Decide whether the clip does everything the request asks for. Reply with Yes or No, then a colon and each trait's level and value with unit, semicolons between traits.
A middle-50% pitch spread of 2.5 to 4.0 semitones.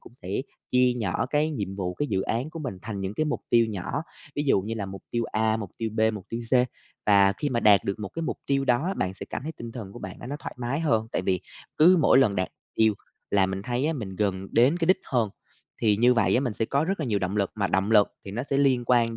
No: average, 5.0 semitones